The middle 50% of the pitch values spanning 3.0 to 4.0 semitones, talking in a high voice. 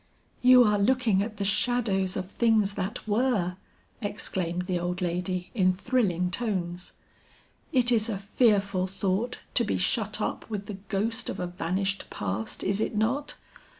Yes: average, 3.6 semitones; high, 200 Hz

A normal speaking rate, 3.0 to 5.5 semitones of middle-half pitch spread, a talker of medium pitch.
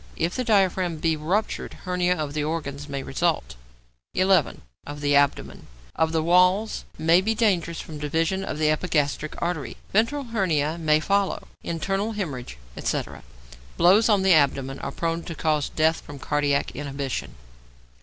Yes: average, 155 wpm; average, 4.2 semitones; medium, 165 Hz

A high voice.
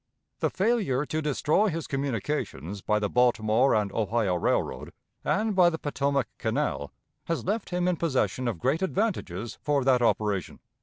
No: low, 135 Hz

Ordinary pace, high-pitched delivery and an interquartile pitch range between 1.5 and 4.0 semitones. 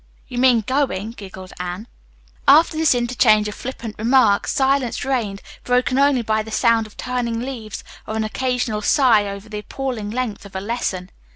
Yes: average, 175 wpm; high, 230 Hz; average, 3.4 semitones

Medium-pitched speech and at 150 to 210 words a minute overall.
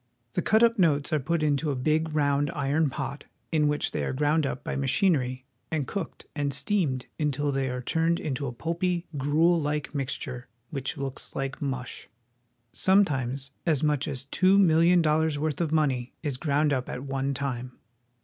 Yes: medium, 145 Hz; average, 180 wpm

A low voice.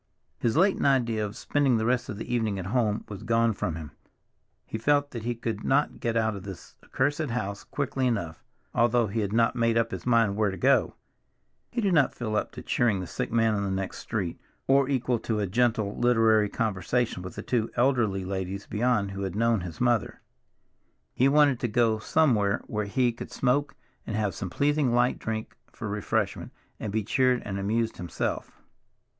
Yes: low, 115 Hz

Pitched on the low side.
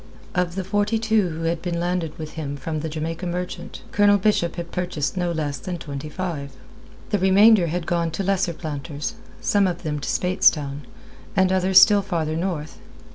No: medium, 175 Hz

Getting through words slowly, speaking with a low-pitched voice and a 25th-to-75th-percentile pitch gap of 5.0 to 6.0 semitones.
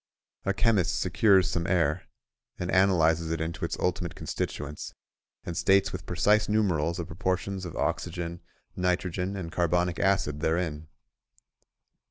No: slow, 130 wpm; very low, 90 Hz; narrow, 2.4 semitones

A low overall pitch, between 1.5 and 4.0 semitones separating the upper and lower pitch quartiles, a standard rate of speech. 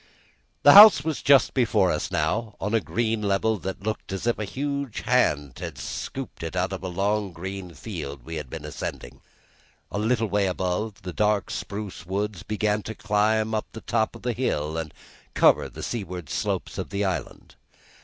Yes: low, 100 Hz; average, 3.6 semitones; average, 185 wpm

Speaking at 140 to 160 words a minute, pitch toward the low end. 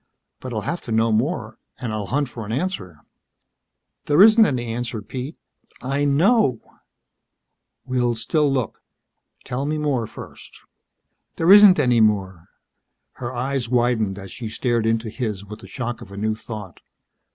Yes: average, 155 wpm; low, 120 Hz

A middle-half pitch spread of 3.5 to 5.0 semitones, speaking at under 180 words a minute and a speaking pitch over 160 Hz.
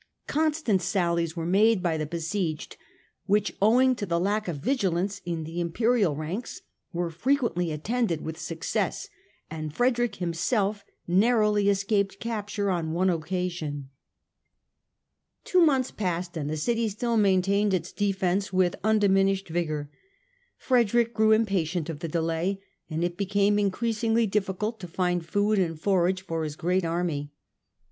Yes: average, 4.0 semitones; average, 140 wpm; high, 190 Hz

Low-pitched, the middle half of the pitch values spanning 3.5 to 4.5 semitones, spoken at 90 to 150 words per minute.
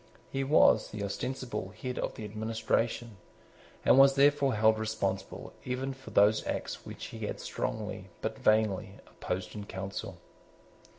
Yes: low, 110 Hz; average, 4.1 semitones; average, 140 wpm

